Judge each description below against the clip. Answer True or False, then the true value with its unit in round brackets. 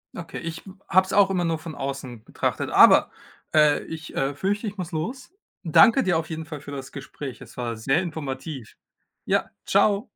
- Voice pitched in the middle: True (160 Hz)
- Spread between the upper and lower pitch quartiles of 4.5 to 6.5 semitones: True (5.3 semitones)